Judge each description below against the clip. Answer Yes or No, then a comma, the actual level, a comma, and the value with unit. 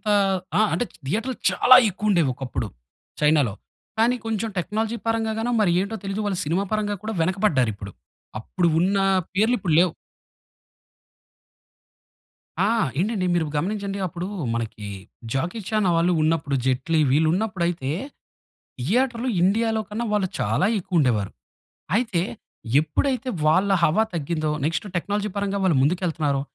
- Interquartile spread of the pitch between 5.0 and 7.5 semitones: Yes, wide, 5.6 semitones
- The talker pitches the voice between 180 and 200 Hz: Yes, medium, 185 Hz